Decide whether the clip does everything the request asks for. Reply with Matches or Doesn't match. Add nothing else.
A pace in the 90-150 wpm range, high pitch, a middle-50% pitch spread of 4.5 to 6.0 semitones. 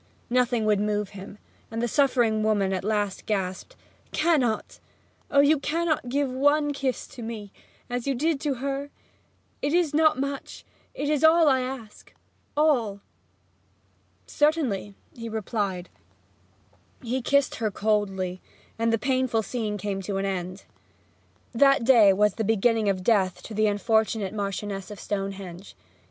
Matches